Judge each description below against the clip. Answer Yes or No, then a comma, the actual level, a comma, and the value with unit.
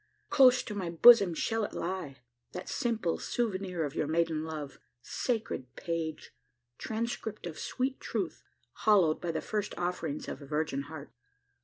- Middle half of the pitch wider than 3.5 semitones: Yes, wide, 5.5 semitones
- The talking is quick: No, average, 150 wpm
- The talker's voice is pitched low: No, medium, 175 Hz